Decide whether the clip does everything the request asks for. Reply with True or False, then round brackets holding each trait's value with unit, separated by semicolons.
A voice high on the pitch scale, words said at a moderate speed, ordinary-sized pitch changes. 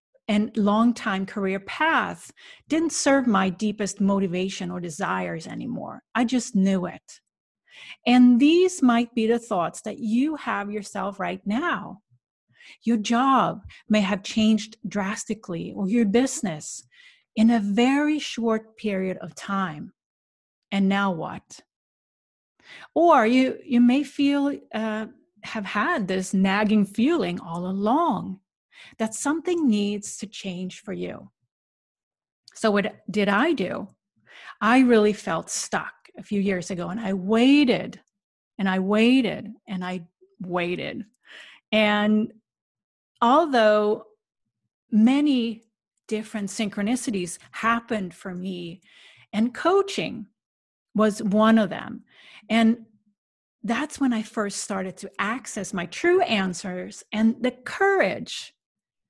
False (215 Hz; 120 wpm; 3.5 semitones)